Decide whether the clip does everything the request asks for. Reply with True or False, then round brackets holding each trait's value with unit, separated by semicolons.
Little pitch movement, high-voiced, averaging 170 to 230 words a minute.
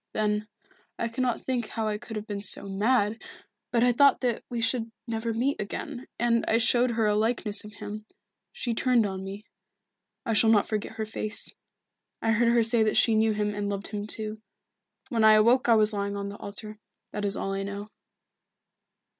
True (2.0 semitones; 220 Hz; 200 wpm)